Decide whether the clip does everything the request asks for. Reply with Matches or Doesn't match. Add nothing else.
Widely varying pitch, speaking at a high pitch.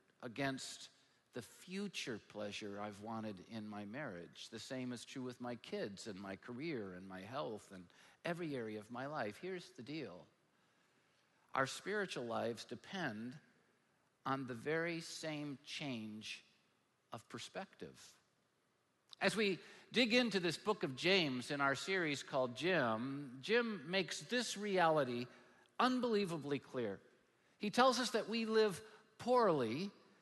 Doesn't match